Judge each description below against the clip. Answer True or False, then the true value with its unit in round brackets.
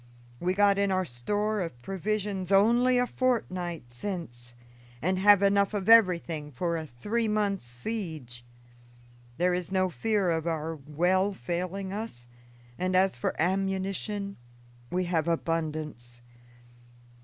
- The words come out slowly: True (130 wpm)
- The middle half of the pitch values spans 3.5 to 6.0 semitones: True (4.0 semitones)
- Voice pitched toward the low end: False (185 Hz)